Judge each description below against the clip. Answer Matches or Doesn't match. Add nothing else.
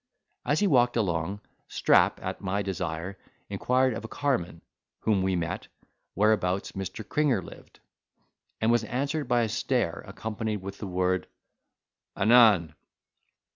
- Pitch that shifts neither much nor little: Matches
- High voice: Doesn't match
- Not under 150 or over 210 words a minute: Doesn't match